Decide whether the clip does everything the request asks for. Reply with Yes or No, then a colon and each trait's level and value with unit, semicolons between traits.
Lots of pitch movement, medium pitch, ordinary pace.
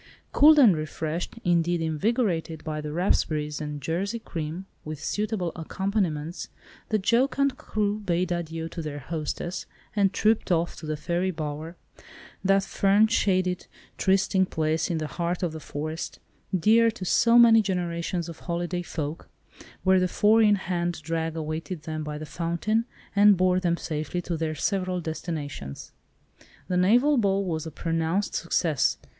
No: average, 3.6 semitones; medium, 175 Hz; average, 150 wpm